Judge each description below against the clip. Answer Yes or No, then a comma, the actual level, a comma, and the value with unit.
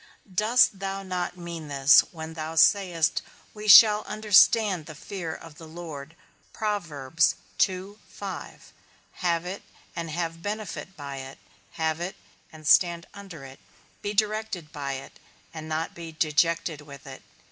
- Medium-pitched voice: Yes, medium, 170 Hz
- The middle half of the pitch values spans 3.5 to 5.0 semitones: Yes, average, 3.9 semitones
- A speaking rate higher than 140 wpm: No, slow, 135 wpm